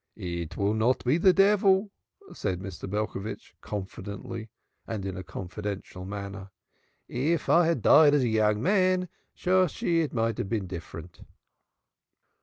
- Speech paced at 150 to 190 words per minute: No, average, 140 wpm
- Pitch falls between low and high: No, low, 110 Hz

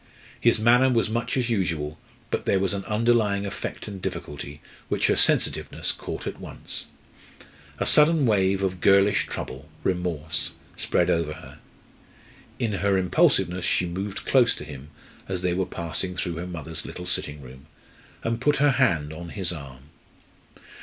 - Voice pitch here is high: No, very low, 95 Hz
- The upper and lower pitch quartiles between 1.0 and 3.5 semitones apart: No, average, 5.0 semitones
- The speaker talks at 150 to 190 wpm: Yes, average, 160 wpm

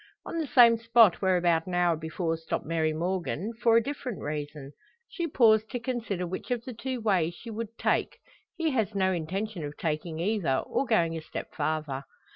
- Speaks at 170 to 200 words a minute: Yes, average, 195 wpm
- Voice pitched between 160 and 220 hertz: Yes, high, 190 Hz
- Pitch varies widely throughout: Yes, wide, 6.0 semitones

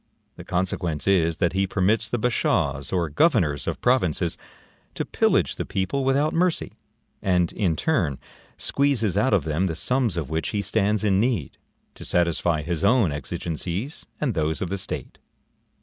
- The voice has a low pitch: Yes, very low, 95 Hz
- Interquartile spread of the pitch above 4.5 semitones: Yes, wide, 5.6 semitones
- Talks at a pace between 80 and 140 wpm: No, average, 165 wpm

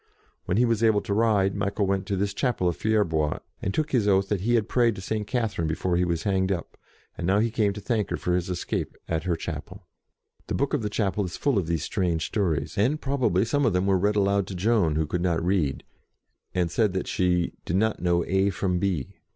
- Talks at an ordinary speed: No, fast, 240 wpm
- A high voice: No, very low, 95 Hz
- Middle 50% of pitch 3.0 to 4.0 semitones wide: Yes, average, 3.4 semitones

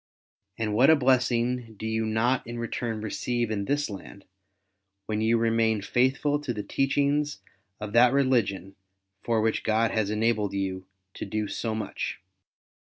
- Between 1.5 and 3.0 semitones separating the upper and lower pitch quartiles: Yes, average, 2.7 semitones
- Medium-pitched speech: No, low, 115 Hz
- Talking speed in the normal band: Yes, average, 150 wpm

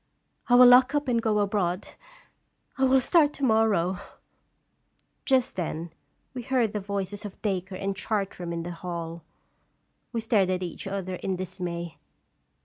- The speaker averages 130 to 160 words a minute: Yes, average, 155 wpm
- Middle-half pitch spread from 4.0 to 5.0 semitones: Yes, average, 4.6 semitones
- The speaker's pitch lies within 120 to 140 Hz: No, high, 195 Hz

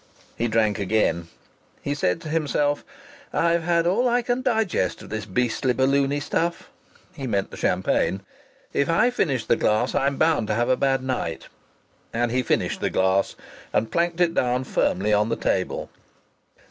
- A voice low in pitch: Yes, low, 130 Hz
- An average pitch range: No, wide, 7.3 semitones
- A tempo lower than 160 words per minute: No, average, 170 wpm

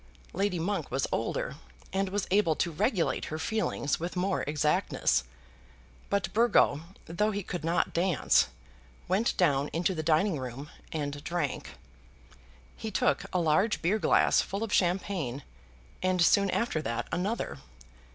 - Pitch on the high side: No, medium, 175 Hz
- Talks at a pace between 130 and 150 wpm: Yes, average, 140 wpm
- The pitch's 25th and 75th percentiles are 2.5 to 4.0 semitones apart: No, average, 4.5 semitones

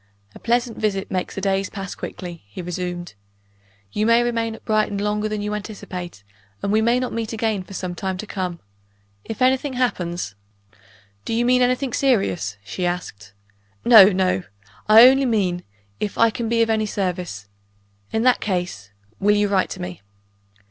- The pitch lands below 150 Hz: No, high, 205 Hz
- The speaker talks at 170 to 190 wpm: Yes, average, 175 wpm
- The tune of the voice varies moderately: Yes, average, 4.3 semitones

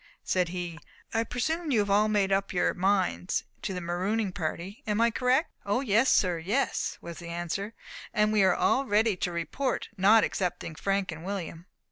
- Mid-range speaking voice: No, high, 200 Hz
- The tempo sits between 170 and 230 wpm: Yes, average, 185 wpm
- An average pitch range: Yes, average, 3.9 semitones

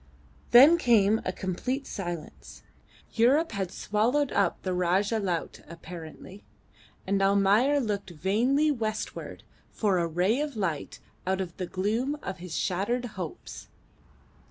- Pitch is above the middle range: Yes, high, 200 Hz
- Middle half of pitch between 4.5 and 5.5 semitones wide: Yes, average, 4.8 semitones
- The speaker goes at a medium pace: No, slow, 130 wpm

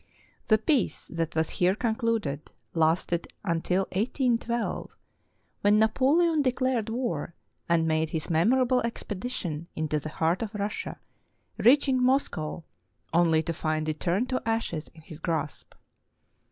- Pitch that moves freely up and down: Yes, wide, 6.9 semitones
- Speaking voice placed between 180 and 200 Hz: Yes, high, 190 Hz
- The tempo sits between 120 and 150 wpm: Yes, slow, 135 wpm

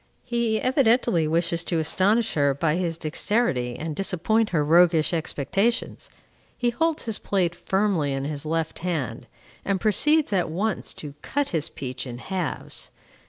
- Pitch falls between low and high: Yes, medium, 175 Hz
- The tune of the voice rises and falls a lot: Yes, wide, 6.0 semitones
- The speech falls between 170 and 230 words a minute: No, average, 150 wpm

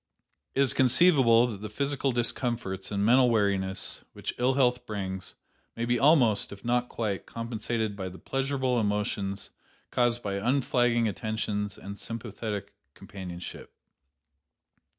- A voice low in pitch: Yes, low, 115 Hz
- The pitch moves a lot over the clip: No, average, 3.5 semitones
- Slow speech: Yes, slow, 130 wpm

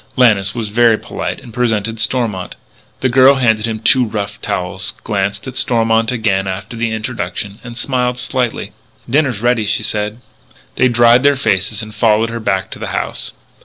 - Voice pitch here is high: No, low, 115 Hz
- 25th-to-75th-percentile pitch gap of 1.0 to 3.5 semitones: Yes, average, 2.8 semitones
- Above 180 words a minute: No, average, 170 wpm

